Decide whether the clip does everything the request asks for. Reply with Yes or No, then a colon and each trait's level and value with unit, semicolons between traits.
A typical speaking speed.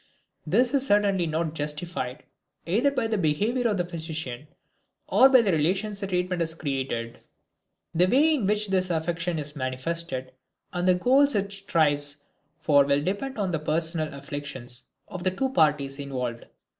Yes: average, 160 wpm